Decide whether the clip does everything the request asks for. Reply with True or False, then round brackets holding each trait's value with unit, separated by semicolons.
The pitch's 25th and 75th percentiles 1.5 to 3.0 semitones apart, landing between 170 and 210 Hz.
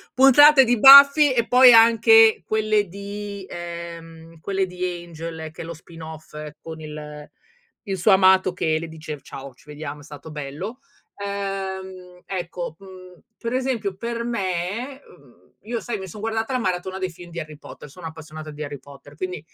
False (5.3 semitones; 185 Hz)